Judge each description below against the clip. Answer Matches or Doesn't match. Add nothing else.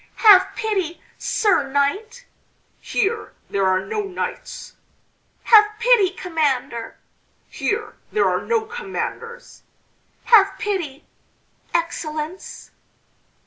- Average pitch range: Doesn't match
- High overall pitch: Matches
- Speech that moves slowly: Matches